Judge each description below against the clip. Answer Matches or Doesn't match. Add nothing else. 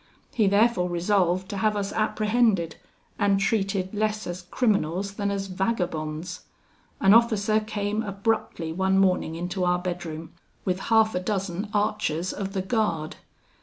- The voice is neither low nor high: Doesn't match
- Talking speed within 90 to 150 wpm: Matches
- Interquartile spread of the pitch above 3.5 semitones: Doesn't match